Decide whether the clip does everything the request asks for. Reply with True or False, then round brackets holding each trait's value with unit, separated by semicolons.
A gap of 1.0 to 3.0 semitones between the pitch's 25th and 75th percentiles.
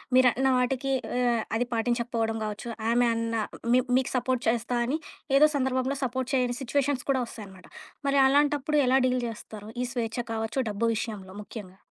True (2.6 semitones)